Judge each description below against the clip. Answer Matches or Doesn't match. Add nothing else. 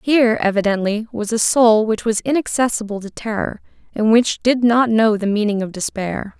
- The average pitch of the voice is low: Doesn't match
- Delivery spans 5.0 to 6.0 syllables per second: Matches